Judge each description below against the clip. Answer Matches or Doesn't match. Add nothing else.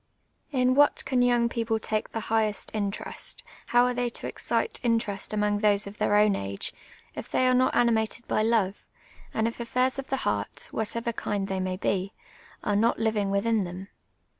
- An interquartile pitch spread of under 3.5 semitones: Matches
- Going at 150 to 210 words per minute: Matches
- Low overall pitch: Doesn't match